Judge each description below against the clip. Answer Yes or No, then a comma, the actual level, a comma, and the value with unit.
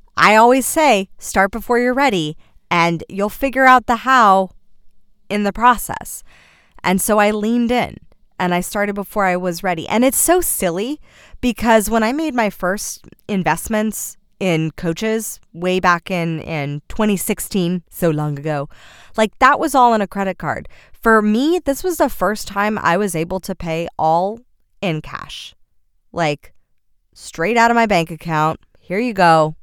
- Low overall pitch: No, high, 200 Hz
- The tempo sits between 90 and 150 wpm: No, average, 165 wpm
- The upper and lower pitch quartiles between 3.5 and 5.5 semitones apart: Yes, average, 5.2 semitones